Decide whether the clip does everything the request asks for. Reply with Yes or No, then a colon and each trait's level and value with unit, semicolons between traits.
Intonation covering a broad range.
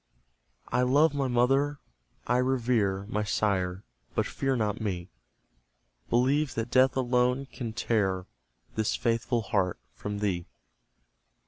No: average, 4.0 semitones